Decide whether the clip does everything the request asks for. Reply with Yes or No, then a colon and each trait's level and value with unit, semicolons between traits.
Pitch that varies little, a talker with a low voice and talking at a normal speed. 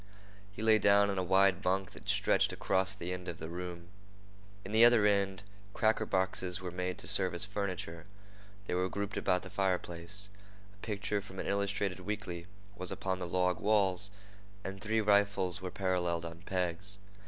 Yes: narrow, 2.0 semitones; very low, 95 Hz; average, 175 wpm